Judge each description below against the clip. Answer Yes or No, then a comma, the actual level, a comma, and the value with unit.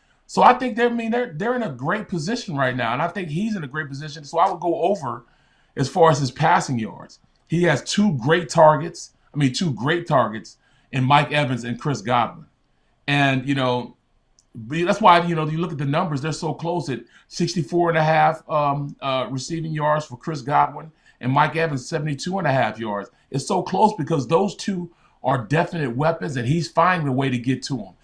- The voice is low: No, medium, 155 Hz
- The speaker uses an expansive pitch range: No, average, 4.0 semitones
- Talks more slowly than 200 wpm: No, fast, 205 wpm